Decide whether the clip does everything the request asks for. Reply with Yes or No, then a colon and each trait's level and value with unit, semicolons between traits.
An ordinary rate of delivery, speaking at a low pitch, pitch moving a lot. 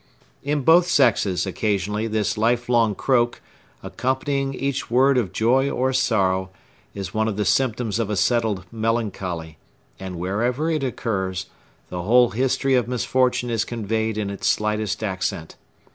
No: average, 145 wpm; low, 115 Hz; average, 4.1 semitones